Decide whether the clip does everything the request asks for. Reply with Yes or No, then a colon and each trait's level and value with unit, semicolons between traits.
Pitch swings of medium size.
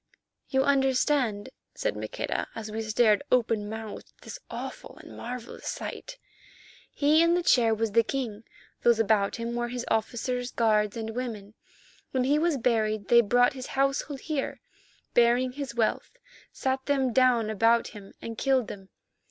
Yes: average, 3.2 semitones